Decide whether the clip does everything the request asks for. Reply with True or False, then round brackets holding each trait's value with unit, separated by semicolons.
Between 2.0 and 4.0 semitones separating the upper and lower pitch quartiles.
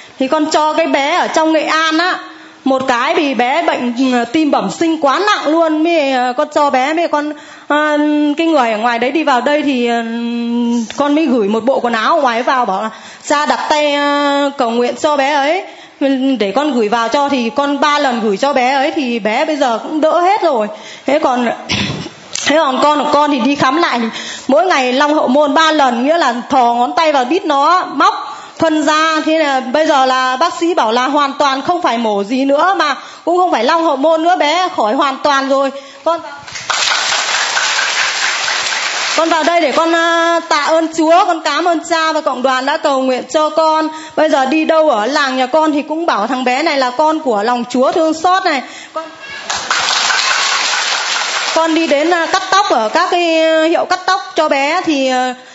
True (3.5 semitones)